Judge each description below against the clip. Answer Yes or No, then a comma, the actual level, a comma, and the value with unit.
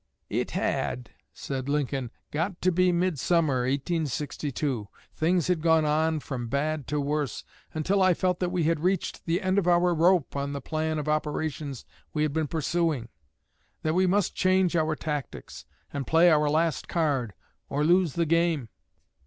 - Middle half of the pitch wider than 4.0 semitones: No, average, 3.3 semitones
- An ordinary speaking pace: Yes, average, 165 wpm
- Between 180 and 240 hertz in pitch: No, medium, 155 Hz